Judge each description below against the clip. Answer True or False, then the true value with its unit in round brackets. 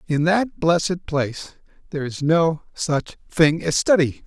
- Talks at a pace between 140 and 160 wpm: True (155 wpm)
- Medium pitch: True (160 Hz)